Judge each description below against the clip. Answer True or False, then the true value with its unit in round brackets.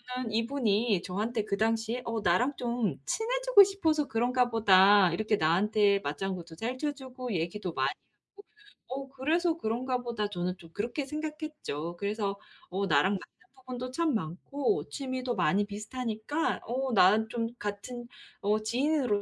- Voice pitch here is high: True (230 Hz)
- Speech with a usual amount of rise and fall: True (4.7 semitones)